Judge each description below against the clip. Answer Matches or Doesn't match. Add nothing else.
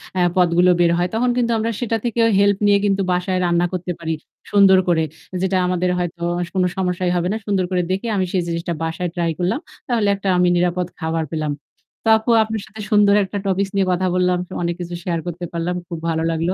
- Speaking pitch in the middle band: Matches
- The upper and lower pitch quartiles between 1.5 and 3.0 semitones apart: Matches